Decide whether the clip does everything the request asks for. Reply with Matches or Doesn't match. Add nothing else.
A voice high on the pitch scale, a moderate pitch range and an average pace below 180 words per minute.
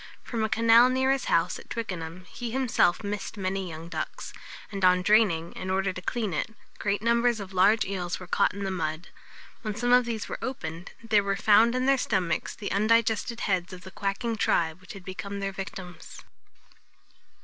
Doesn't match